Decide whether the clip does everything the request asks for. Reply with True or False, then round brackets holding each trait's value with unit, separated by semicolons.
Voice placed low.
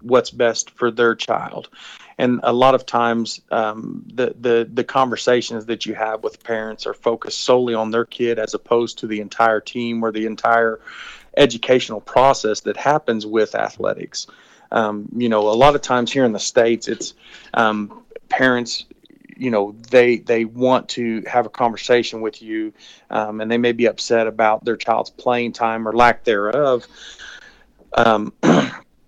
True (115 Hz)